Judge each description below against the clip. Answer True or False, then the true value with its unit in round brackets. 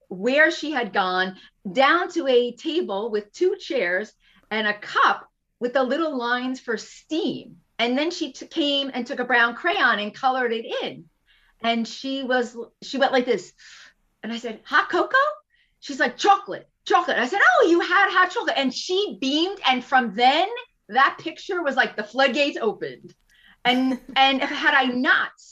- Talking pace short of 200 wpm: True (180 wpm)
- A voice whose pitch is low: False (270 Hz)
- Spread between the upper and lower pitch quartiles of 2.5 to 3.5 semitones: False (5.3 semitones)